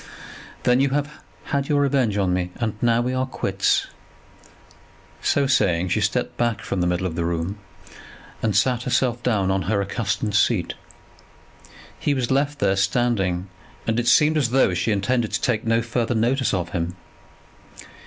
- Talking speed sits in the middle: Yes, average, 170 wpm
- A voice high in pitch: No, low, 115 Hz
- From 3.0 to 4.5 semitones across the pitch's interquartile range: No, average, 4.9 semitones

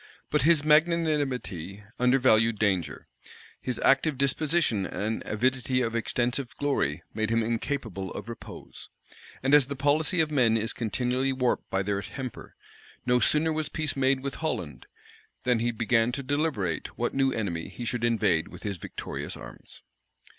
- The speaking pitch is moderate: No, low, 125 Hz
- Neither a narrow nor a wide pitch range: Yes, average, 4.4 semitones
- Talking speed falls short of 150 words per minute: No, average, 155 wpm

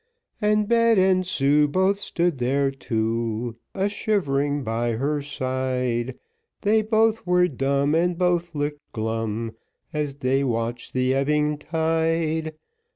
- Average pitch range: No, wide, 5.7 semitones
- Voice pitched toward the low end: No, medium, 145 Hz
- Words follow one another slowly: Yes, slow, 125 wpm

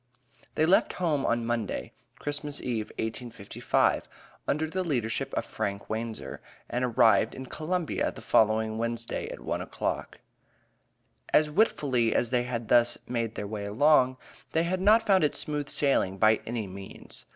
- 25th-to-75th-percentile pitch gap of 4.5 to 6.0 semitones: Yes, average, 5.2 semitones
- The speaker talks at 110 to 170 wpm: Yes, average, 150 wpm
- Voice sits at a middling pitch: No, low, 120 Hz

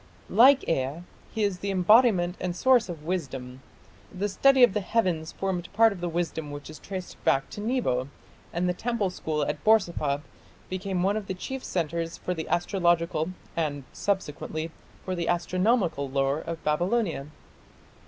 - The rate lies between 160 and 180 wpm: Yes, average, 165 wpm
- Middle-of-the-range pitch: Yes, medium, 175 Hz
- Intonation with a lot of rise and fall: No, average, 4.1 semitones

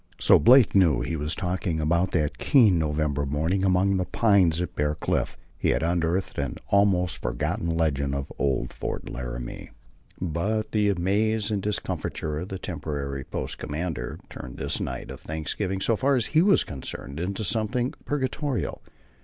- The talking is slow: No, average, 165 wpm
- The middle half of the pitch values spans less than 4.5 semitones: No, average, 5.3 semitones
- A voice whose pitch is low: Yes, very low, 90 Hz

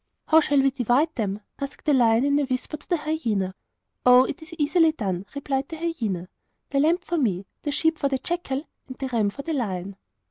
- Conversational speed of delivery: No, fast, 215 wpm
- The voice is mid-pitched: No, very high, 275 Hz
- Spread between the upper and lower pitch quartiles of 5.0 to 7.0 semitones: Yes, wide, 5.4 semitones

